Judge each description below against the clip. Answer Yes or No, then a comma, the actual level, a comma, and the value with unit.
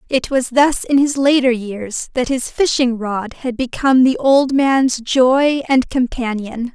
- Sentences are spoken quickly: No, average, 170 wpm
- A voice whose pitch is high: Yes, very high, 255 Hz